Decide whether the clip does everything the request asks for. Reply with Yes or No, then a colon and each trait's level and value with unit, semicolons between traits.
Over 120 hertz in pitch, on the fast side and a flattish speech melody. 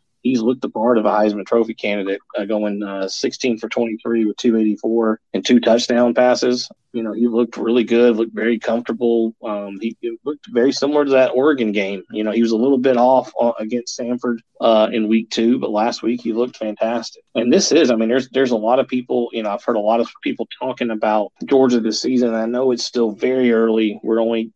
No: low, 115 Hz; fast, 225 wpm; narrow, 1.9 semitones